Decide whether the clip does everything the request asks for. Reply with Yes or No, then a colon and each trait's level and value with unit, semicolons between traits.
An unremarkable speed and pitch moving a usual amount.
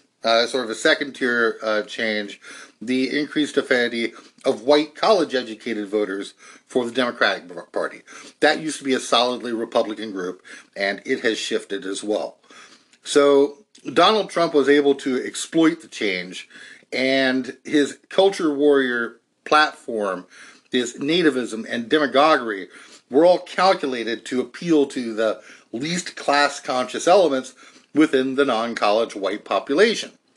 No: slow, 130 wpm; average, 4.1 semitones